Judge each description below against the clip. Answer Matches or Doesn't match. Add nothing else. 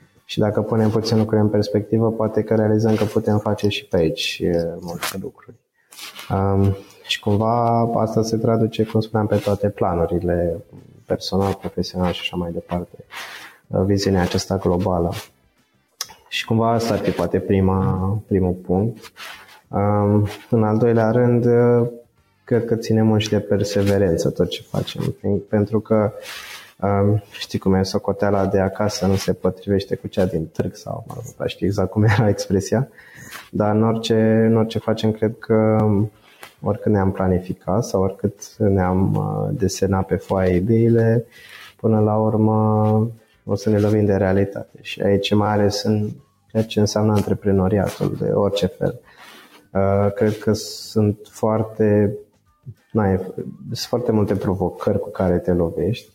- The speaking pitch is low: Matches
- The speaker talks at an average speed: Matches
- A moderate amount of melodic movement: Doesn't match